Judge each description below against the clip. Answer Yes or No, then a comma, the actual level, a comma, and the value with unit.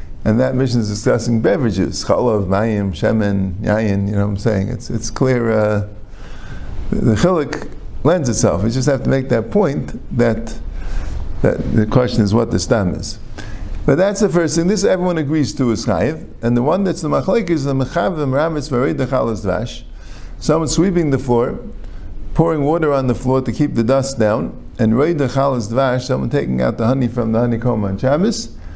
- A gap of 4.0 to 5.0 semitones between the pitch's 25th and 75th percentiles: Yes, average, 4.3 semitones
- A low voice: Yes, low, 120 Hz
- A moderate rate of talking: Yes, average, 185 wpm